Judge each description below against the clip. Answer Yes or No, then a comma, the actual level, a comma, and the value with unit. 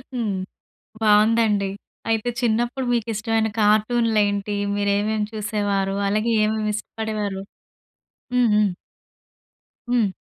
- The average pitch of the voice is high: Yes, high, 215 Hz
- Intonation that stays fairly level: Yes, narrow, 1.5 semitones